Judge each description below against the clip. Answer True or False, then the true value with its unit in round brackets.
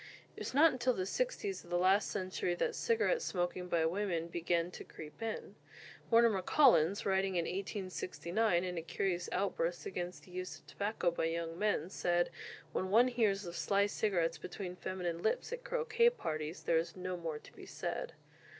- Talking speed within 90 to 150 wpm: False (180 wpm)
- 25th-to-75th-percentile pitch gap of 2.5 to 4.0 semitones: True (3.7 semitones)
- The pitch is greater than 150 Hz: True (185 Hz)